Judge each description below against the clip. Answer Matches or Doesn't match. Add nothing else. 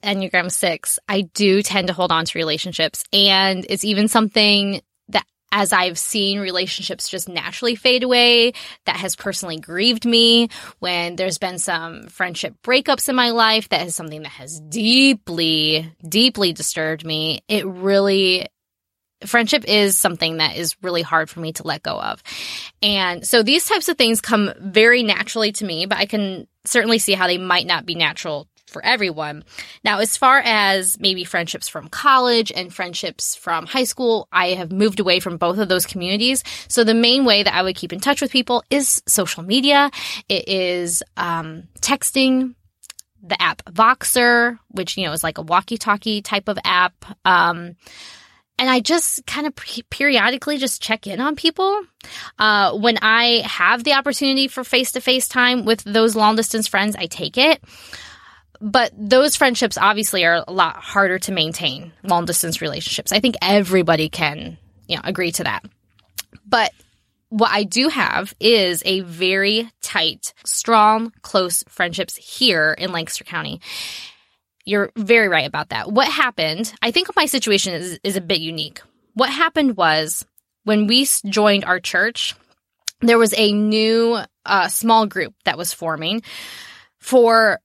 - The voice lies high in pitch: Matches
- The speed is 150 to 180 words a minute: Matches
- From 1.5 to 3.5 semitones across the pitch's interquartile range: Doesn't match